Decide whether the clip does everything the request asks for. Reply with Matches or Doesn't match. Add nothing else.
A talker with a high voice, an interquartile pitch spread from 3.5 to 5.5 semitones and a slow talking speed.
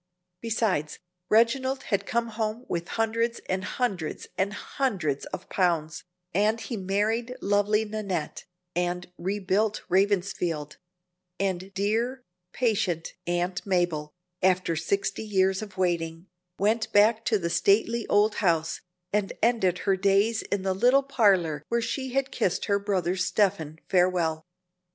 Matches